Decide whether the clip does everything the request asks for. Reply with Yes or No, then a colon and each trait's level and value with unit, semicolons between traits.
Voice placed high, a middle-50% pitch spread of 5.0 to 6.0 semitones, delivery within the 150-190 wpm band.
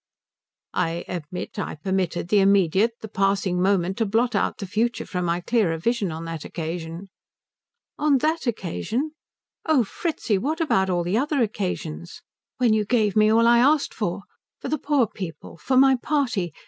Yes: high, 205 Hz; average, 5.3 semitones; average, 170 wpm